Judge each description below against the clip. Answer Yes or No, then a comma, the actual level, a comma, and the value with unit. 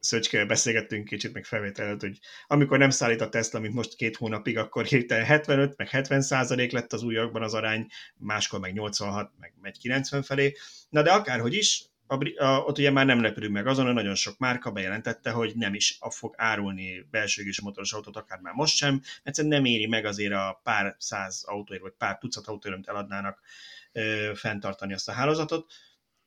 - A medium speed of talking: No, fast, 185 wpm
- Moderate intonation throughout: Yes, average, 4.4 semitones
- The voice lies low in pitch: Yes, low, 115 Hz